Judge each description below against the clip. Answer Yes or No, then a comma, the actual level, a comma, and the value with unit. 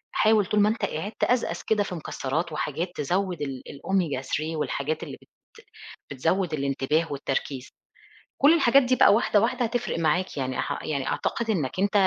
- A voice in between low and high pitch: Yes, medium, 170 Hz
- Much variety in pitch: Yes, wide, 6.7 semitones